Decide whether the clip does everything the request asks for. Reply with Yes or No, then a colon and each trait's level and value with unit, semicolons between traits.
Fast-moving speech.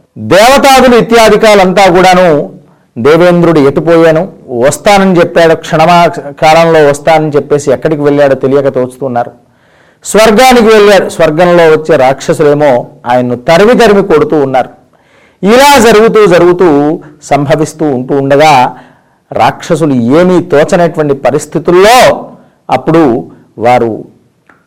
No: average, 90 wpm